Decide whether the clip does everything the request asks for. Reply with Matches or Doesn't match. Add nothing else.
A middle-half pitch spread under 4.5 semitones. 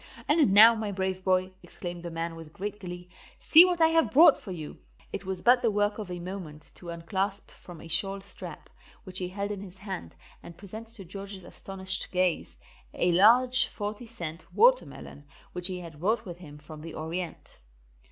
Matches